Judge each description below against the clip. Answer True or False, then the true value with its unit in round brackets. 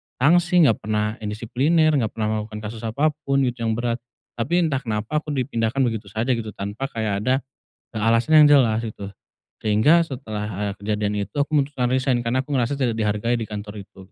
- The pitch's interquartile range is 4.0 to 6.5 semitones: True (4.3 semitones)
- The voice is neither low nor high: False (115 Hz)